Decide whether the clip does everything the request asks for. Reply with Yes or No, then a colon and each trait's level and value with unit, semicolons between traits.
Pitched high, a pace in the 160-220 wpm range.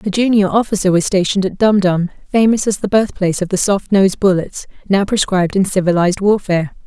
Yes: high, 195 Hz; average, 190 wpm